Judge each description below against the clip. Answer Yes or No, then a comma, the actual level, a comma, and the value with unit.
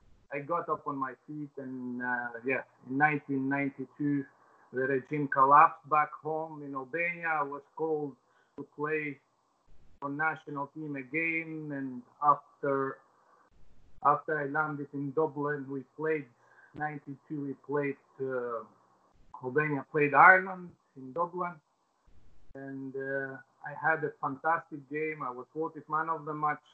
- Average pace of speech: No, slow, 130 wpm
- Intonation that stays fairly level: Yes, narrow, 2.3 semitones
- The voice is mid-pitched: Yes, medium, 145 Hz